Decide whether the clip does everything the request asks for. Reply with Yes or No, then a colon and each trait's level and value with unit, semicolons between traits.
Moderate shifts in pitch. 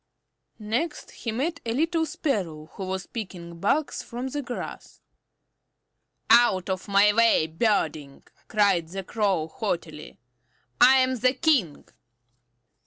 No: wide, 6.2 semitones